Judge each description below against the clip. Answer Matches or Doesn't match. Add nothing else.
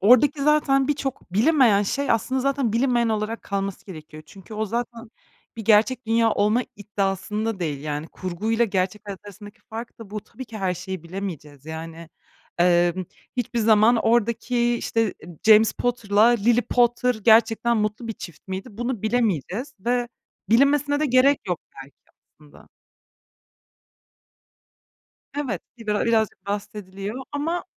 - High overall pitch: Matches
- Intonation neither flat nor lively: Matches